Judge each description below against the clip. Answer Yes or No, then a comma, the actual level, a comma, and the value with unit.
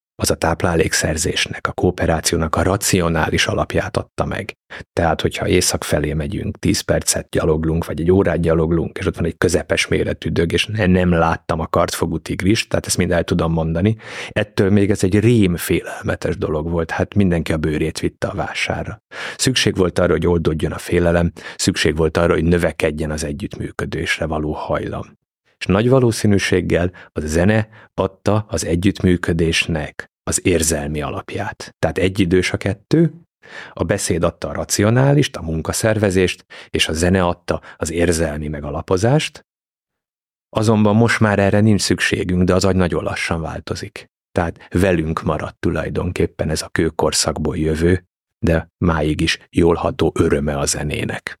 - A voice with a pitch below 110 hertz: Yes, very low, 90 Hz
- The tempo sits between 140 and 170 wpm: Yes, average, 150 wpm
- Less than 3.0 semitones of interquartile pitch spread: No, average, 3.5 semitones